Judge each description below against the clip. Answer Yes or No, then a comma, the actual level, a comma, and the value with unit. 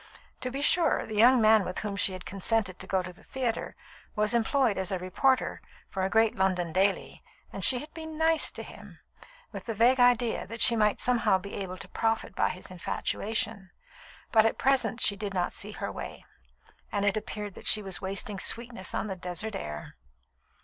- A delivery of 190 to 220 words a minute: Yes, average, 200 wpm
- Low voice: No, high, 210 Hz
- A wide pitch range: No, average, 3.7 semitones